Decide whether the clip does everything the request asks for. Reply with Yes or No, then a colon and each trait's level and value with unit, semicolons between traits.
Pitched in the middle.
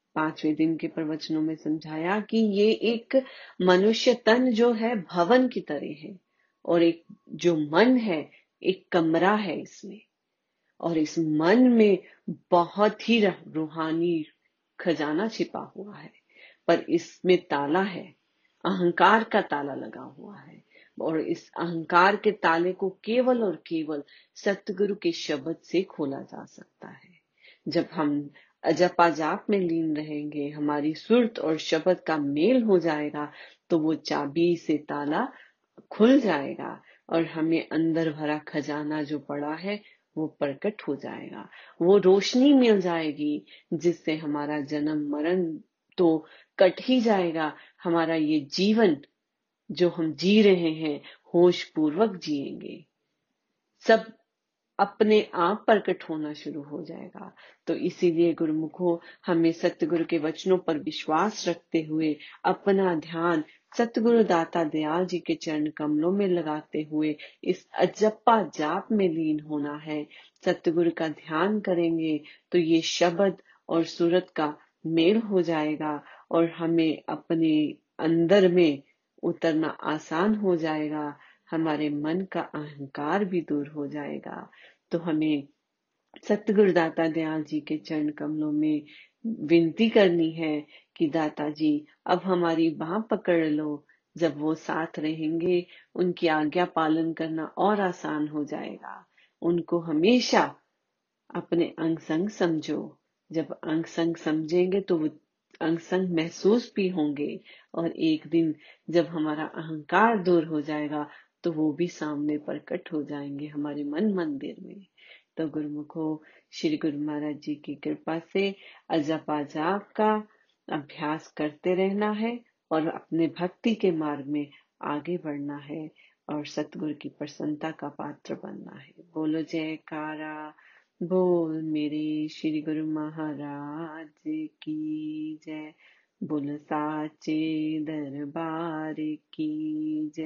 Yes: medium, 165 Hz